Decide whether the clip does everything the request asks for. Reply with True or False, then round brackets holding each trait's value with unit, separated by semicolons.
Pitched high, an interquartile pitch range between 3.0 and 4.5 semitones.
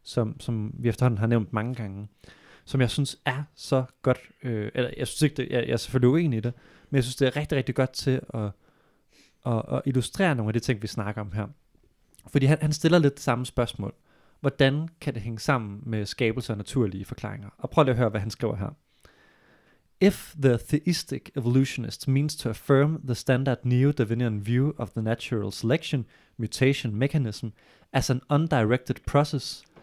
False (125 Hz; 3.5 semitones)